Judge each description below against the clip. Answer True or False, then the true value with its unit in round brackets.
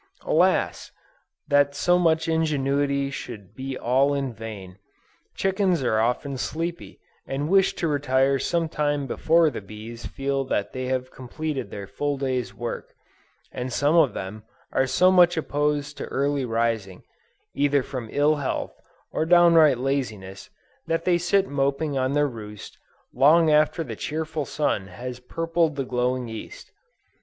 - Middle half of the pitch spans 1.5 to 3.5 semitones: False (3.9 semitones)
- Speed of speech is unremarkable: True (145 wpm)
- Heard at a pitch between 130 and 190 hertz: True (140 Hz)